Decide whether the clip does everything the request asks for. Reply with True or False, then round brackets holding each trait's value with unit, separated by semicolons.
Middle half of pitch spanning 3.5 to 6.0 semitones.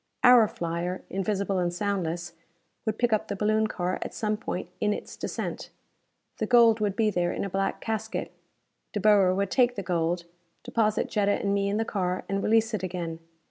False (3.0 semitones)